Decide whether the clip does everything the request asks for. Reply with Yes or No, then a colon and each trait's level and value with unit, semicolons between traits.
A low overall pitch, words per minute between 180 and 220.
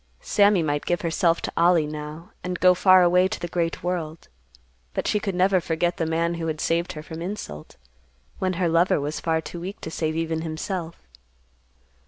No: medium, 170 Hz; average, 195 wpm